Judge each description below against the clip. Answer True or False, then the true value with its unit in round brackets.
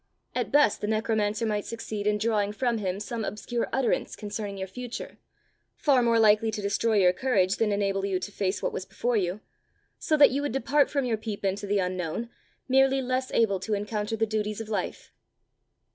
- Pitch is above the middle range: True (215 Hz)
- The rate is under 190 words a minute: False (195 wpm)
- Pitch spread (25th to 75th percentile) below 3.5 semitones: True (2.8 semitones)